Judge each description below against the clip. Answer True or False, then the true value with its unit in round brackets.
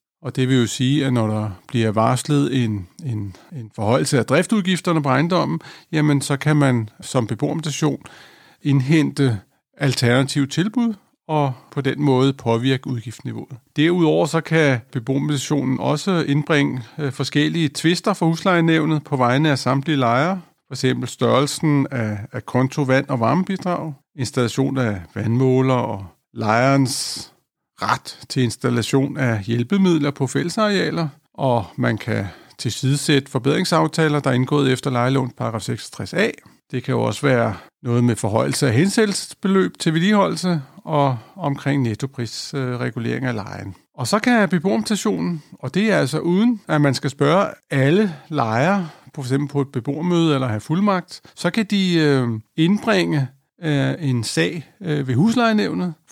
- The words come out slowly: True (135 wpm)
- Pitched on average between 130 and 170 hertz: True (140 Hz)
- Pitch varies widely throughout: False (4.3 semitones)